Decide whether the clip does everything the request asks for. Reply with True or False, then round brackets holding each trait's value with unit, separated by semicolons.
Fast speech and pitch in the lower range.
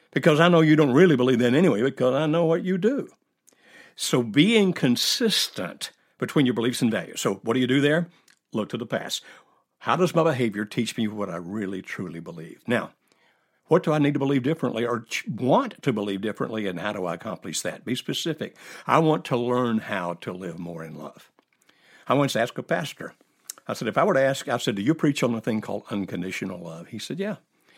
True (220 wpm; 125 Hz)